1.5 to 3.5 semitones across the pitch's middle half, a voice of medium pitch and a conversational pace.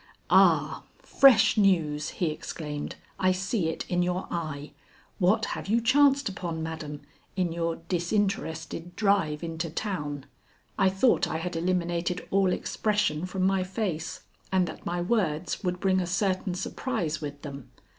Yes: average, 3.2 semitones; medium, 180 Hz; average, 145 wpm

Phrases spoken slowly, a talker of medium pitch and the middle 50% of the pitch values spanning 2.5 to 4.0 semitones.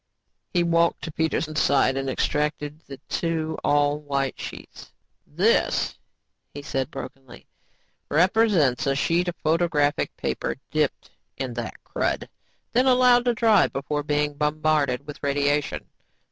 Yes: slow, 130 wpm; medium, 150 Hz; average, 2.9 semitones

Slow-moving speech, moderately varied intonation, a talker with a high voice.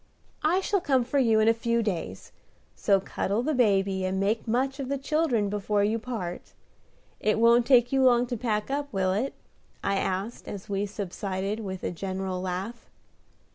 No: average, 180 wpm; average, 4.3 semitones; high, 220 Hz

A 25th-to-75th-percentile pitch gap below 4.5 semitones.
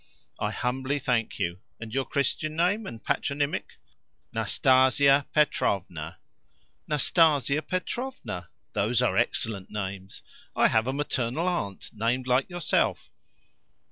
No: average, 5.2 semitones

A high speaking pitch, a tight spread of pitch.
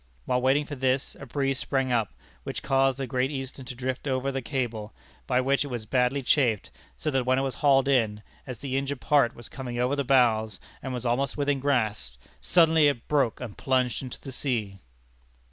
No: low, 130 Hz; narrow, 2.2 semitones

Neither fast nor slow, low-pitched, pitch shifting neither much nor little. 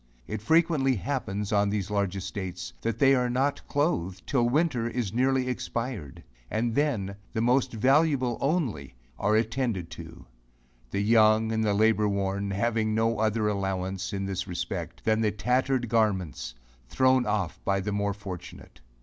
Yes: average, 155 wpm; low, 110 Hz; average, 4.2 semitones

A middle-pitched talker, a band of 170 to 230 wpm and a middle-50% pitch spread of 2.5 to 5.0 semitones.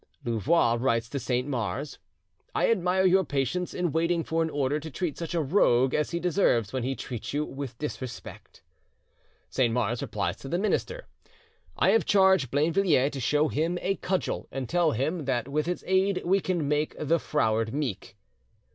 No: medium, 150 Hz; average, 180 wpm; wide, 5.5 semitones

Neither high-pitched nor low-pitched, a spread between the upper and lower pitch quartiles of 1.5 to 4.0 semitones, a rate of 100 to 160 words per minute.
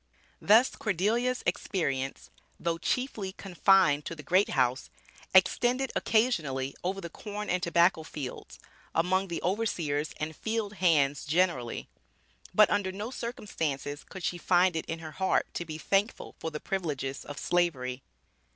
No: medium, 175 Hz; average, 4.9 semitones; average, 140 wpm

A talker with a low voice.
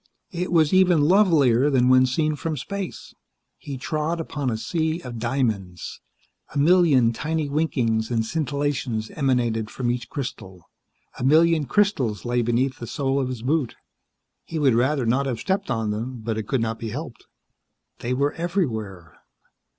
Yes: low, 130 Hz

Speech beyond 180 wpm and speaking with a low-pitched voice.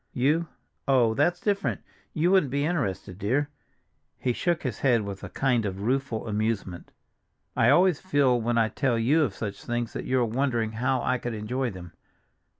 No: average, 175 wpm; low, 125 Hz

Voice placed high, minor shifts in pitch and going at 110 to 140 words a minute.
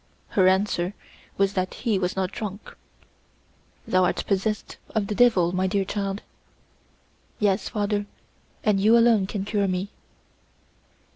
Yes: high, 200 Hz; narrow, 1.9 semitones; slow, 135 wpm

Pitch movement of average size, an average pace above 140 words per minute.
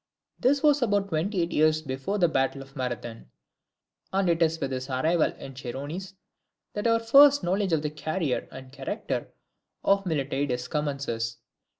No: wide, 6.5 semitones; average, 165 wpm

